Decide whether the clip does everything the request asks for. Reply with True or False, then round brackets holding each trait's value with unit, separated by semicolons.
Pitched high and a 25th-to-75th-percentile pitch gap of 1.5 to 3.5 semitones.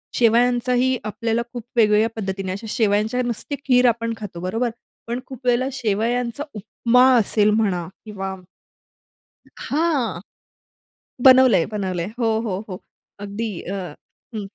True (225 Hz; 3.2 semitones)